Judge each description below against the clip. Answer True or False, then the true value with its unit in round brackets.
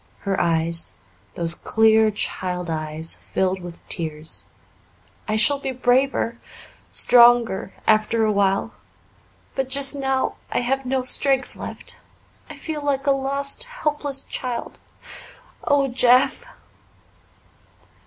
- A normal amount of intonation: False (6.1 semitones)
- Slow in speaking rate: True (115 wpm)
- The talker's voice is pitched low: False (240 Hz)